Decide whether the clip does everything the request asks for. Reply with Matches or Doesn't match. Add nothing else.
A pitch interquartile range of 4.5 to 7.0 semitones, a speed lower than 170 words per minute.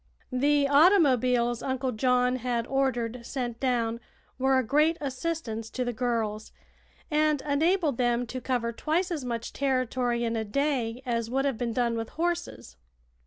Doesn't match